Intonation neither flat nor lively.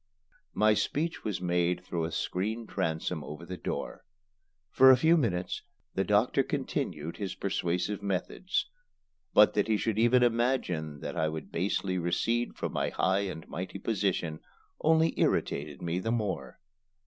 Yes: average, 5.0 semitones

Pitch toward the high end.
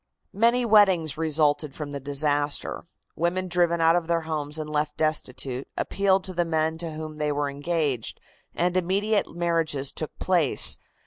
No: medium, 160 Hz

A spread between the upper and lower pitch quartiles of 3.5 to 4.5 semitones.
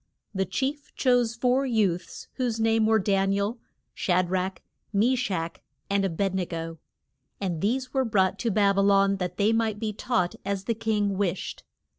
No: average, 3.1 semitones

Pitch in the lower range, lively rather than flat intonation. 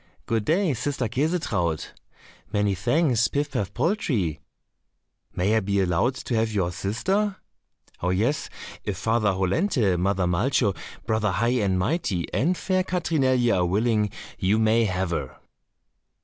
Yes: low, 110 Hz; wide, 6.0 semitones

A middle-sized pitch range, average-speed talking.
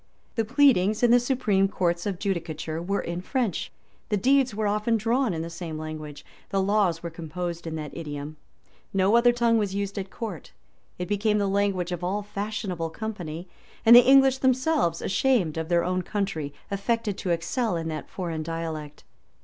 Yes: average, 4.8 semitones; average, 180 wpm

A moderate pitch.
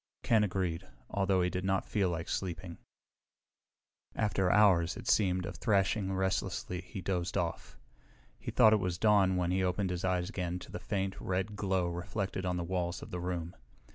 No: very low, 95 Hz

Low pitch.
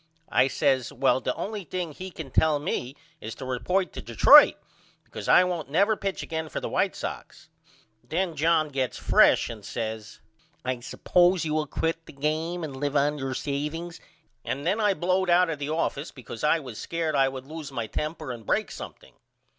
No: medium, 155 Hz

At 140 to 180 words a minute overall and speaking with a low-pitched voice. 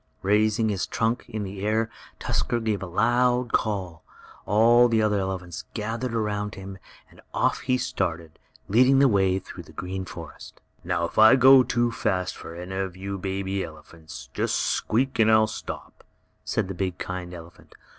Yes: average, 170 wpm; low, 100 Hz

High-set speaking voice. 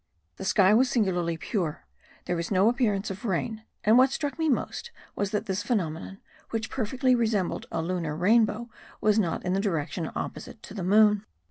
Yes: high, 205 Hz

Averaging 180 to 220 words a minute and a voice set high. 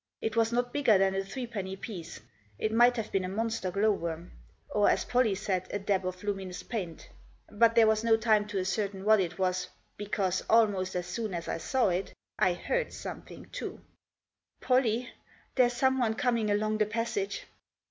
Yes: average, 185 wpm; high, 210 Hz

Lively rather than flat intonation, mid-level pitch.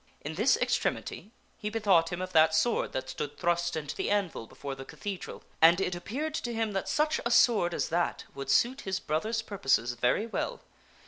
Yes: wide, 5.9 semitones; medium, 180 Hz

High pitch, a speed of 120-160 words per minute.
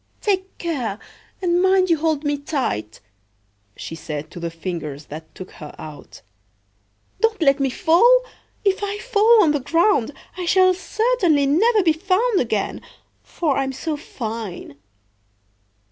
Yes: very high, 315 Hz; average, 145 wpm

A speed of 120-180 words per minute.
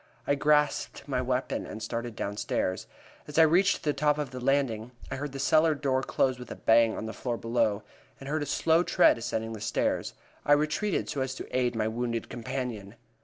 No: fast, 205 wpm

